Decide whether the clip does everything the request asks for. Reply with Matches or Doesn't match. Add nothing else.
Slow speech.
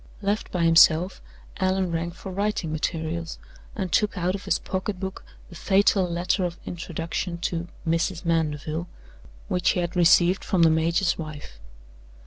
Doesn't match